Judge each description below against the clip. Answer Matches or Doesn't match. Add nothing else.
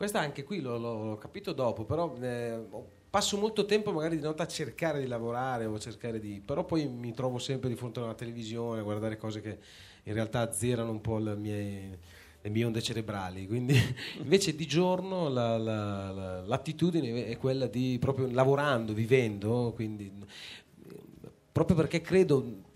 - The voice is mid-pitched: Doesn't match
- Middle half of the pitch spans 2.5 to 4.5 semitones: Doesn't match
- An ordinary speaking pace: Doesn't match